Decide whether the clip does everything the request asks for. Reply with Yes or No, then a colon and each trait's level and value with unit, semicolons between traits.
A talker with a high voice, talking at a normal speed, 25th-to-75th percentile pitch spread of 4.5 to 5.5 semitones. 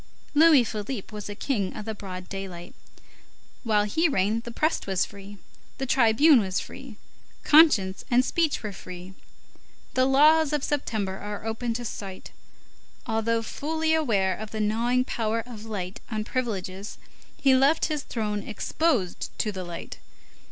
Yes: high, 220 Hz; average, 150 wpm; average, 5.0 semitones